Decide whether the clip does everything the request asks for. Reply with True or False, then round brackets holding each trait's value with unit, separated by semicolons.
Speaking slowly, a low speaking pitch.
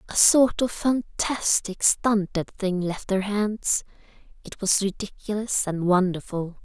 False (125 wpm; 200 Hz)